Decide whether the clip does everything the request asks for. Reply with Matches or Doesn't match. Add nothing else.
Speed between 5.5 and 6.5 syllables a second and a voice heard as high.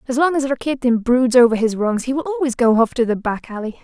Matches